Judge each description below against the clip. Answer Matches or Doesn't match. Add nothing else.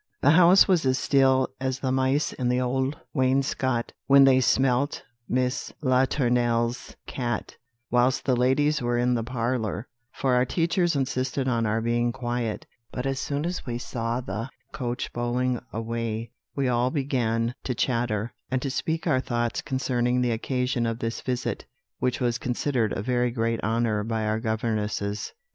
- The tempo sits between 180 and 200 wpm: Doesn't match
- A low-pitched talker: Matches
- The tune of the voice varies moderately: Doesn't match